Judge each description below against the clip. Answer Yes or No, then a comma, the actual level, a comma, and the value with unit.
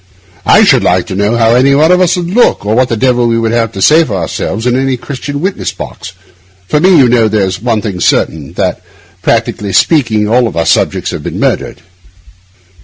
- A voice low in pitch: Yes, low, 120 Hz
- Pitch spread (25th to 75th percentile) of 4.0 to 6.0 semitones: Yes, average, 4.8 semitones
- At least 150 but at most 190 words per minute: No, fast, 205 wpm